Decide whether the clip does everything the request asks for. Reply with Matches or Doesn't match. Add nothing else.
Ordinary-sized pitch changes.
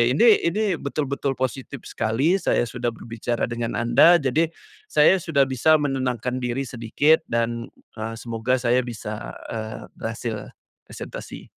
Matches